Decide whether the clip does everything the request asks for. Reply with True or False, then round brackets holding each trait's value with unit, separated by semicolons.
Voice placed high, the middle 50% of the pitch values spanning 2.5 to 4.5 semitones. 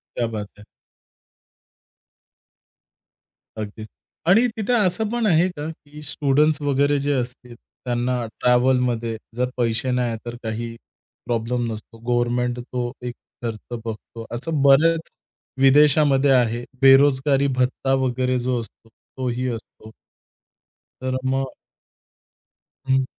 False (125 Hz; 3.0 semitones)